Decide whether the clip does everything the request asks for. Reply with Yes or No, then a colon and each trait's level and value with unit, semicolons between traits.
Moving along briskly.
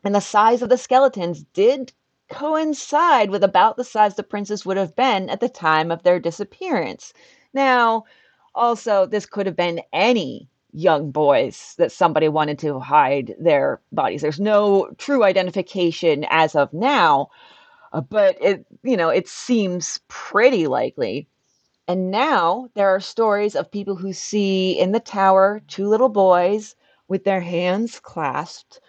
No: average, 150 wpm